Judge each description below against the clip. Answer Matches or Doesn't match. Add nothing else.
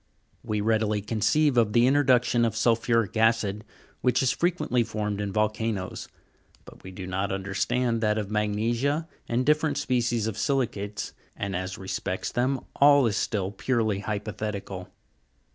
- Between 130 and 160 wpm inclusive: Matches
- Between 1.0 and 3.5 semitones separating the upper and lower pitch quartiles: Matches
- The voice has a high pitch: Doesn't match